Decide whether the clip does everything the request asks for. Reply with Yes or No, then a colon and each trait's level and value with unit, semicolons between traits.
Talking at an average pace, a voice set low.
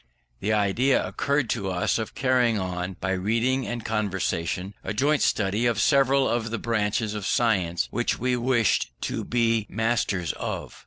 Yes: average, 160 wpm; low, 110 Hz